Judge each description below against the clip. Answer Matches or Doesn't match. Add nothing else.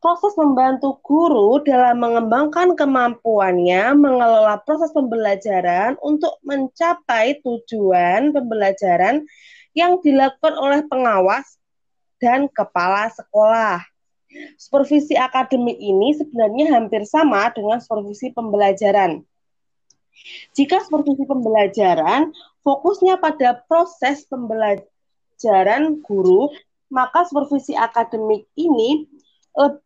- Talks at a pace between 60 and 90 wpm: Matches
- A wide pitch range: Matches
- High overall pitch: Matches